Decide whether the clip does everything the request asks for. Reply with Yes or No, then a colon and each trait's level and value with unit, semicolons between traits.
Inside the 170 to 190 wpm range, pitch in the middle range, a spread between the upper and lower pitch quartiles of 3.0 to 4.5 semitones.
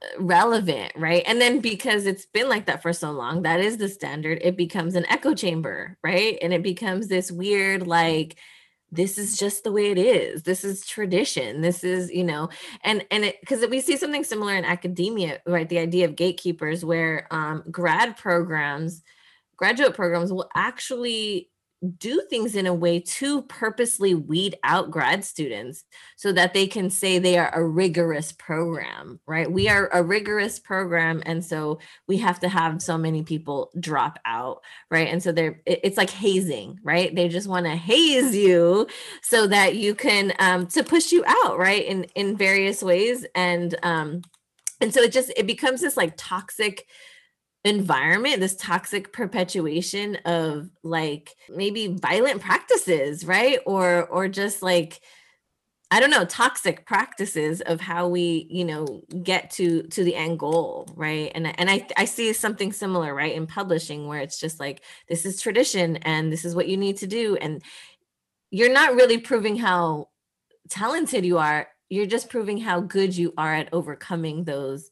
Yes: average, 175 wpm; medium, 180 Hz; average, 3.7 semitones